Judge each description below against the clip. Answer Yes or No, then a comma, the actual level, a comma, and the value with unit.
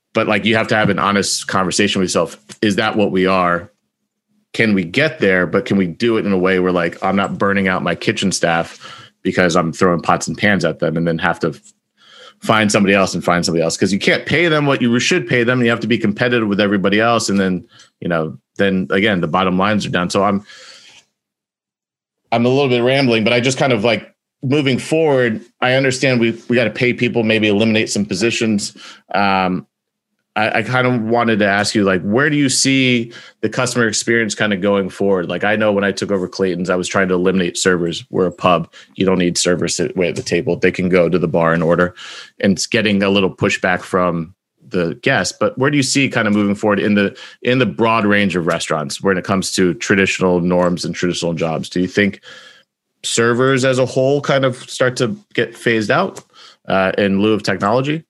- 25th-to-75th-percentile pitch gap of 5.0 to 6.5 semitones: No, average, 4.5 semitones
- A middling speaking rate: No, fast, 225 wpm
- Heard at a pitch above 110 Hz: No, low, 100 Hz